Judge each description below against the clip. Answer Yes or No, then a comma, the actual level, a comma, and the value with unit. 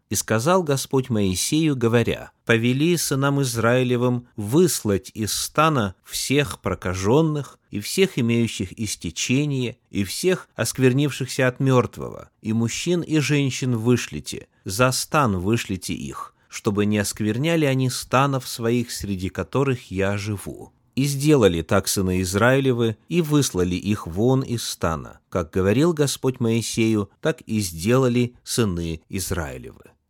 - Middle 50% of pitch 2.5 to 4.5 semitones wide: No, average, 4.9 semitones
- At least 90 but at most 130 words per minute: Yes, average, 120 wpm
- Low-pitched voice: Yes, low, 120 Hz